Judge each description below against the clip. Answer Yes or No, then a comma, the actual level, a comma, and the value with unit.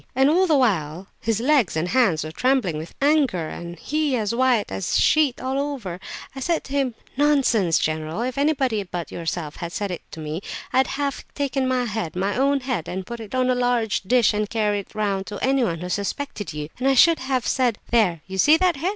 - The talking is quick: Yes, fast, 225 wpm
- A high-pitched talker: Yes, high, 235 Hz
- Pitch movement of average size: No, wide, 6.9 semitones